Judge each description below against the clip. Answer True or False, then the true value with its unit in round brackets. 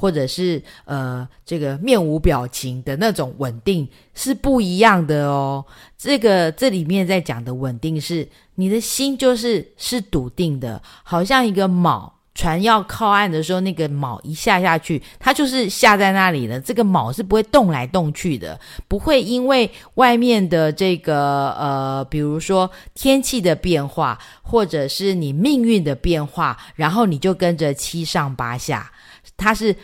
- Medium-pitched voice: True (175 Hz)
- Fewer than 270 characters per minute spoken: True (235 characters per minute)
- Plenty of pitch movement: True (7.1 semitones)